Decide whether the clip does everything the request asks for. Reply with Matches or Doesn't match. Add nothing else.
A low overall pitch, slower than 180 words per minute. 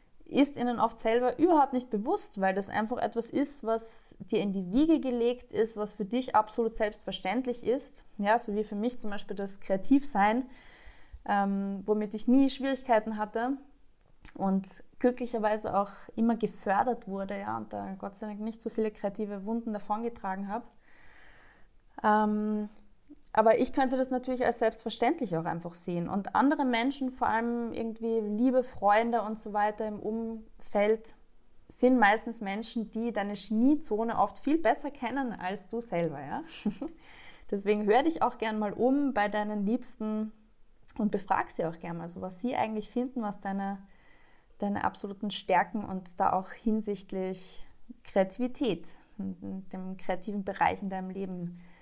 Doesn't match